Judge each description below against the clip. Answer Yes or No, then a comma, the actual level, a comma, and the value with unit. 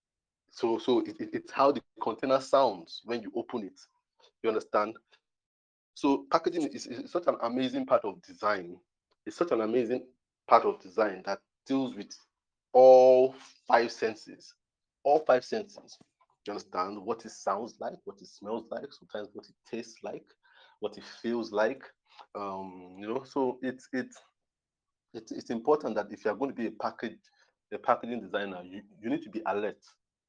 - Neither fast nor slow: Yes, average, 170 wpm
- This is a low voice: Yes, low, 130 Hz